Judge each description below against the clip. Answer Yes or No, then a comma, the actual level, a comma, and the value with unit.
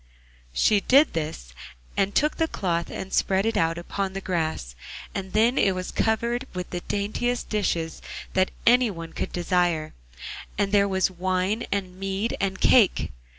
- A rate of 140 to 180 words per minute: Yes, average, 165 wpm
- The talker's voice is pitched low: No, high, 190 Hz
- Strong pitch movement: No, average, 3.2 semitones